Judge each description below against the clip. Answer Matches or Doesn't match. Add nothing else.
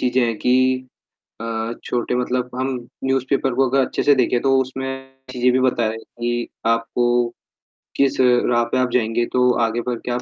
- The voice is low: Matches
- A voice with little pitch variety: Matches